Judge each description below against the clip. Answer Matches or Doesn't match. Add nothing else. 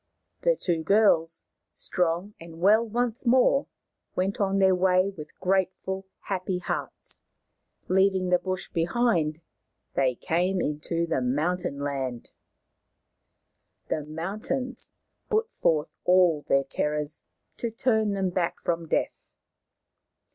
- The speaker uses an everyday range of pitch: Matches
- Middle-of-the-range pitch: Matches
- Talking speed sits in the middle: Doesn't match